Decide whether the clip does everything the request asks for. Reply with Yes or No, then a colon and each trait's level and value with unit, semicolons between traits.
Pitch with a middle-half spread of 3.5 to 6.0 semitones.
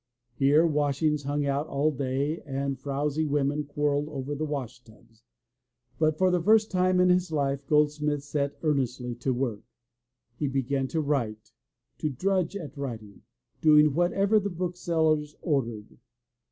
No: narrow, 2.6 semitones